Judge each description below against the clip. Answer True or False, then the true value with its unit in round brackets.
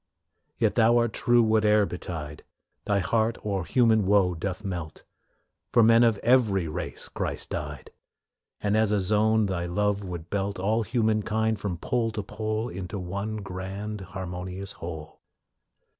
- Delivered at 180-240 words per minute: False (150 wpm)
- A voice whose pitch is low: True (105 Hz)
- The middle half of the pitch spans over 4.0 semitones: False (3.0 semitones)